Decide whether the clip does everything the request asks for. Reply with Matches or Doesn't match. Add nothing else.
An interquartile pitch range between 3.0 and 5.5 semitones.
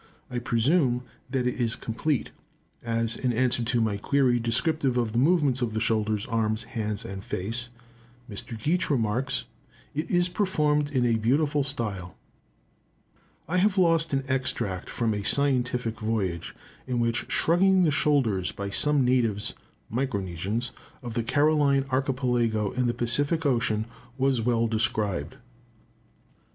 Matches